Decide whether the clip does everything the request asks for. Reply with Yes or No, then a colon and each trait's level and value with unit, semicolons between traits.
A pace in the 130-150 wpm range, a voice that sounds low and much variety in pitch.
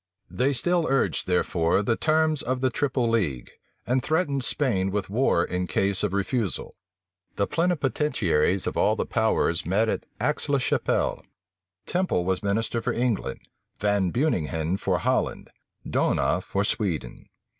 Yes: average, 145 wpm; low, 115 Hz; wide, 6.4 semitones